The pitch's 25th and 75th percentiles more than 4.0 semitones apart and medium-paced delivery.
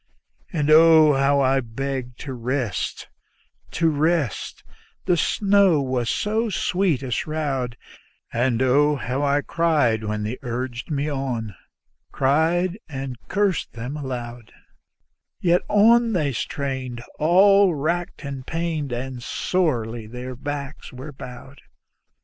No: average, 4.6 semitones; slow, 120 wpm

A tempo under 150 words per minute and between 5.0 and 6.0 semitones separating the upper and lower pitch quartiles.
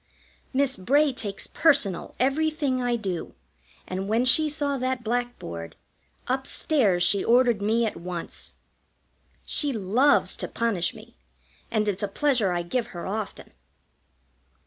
Yes: slow, 135 wpm; wide, 5.4 semitones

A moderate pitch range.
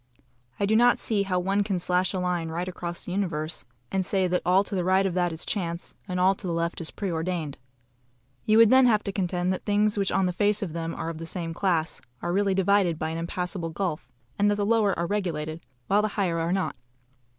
Yes: average, 3.0 semitones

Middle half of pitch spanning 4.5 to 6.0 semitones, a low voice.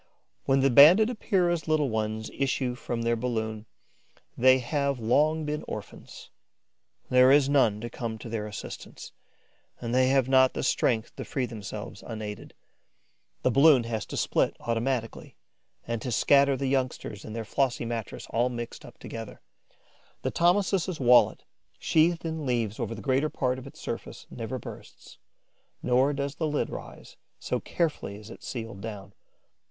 No: average, 3.6 semitones; low, 125 Hz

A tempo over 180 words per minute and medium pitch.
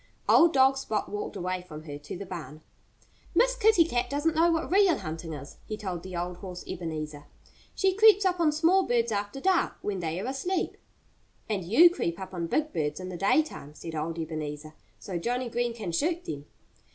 No: average, 200 wpm; high, 200 Hz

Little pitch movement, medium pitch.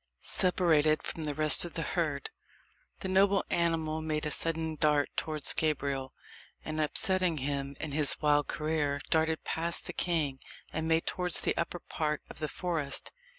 Yes: narrow, 1.9 semitones; medium, 155 Hz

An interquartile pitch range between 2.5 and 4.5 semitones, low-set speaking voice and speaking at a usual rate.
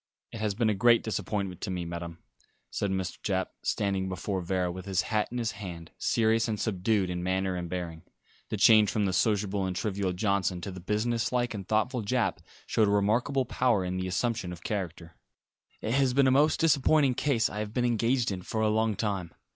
No: average, 3.7 semitones; low, 105 Hz; fast, 210 wpm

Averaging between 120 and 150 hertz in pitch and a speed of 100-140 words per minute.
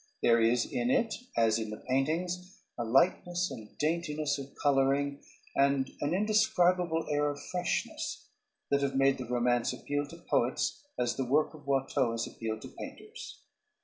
No: medium, 140 Hz; average, 160 wpm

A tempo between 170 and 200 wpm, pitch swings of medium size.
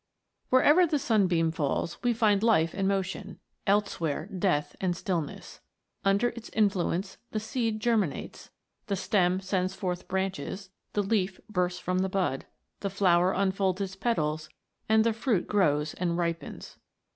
No: average, 145 wpm; average, 3.0 semitones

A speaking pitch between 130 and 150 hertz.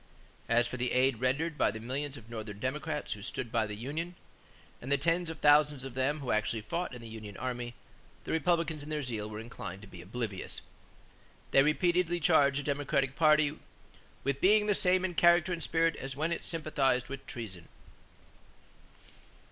Yes: medium, 140 Hz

